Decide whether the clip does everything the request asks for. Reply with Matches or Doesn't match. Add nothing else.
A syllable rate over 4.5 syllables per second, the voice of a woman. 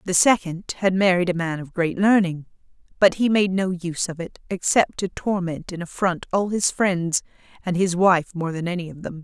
Matches